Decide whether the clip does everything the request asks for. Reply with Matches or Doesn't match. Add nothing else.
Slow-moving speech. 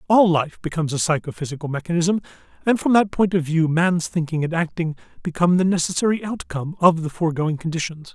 Doesn't match